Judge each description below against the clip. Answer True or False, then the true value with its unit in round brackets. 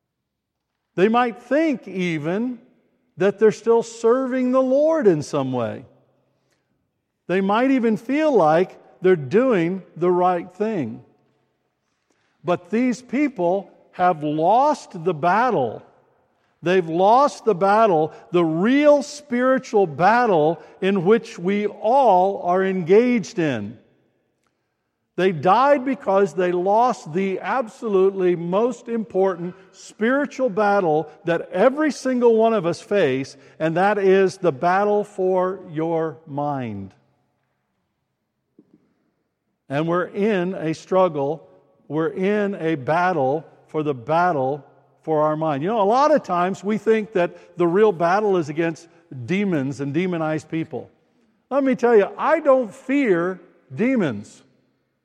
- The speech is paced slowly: True (120 wpm)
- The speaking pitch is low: False (190 Hz)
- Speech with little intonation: False (5.2 semitones)